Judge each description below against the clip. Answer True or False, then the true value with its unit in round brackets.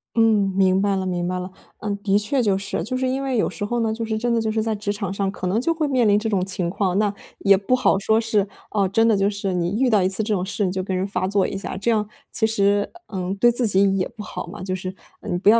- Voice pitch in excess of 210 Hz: False (205 Hz)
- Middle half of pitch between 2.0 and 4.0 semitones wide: True (2.7 semitones)